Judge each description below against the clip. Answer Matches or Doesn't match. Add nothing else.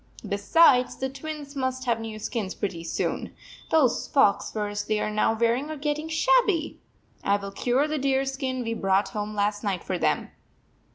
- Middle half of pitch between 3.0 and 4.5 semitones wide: Doesn't match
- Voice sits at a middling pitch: Doesn't match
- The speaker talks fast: Doesn't match